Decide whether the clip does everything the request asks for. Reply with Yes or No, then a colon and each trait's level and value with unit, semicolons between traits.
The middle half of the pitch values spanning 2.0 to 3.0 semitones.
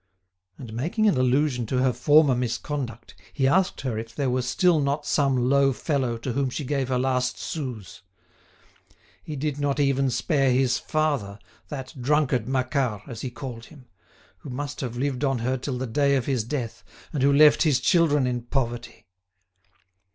Yes: narrow, 2.6 semitones